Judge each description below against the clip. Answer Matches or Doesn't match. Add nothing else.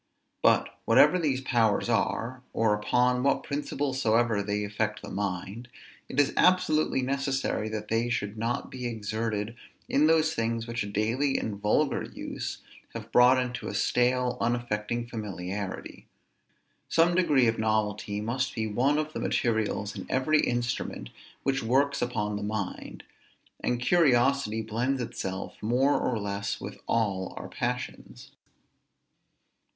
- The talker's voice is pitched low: Matches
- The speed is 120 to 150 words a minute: Matches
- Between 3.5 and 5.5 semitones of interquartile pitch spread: Matches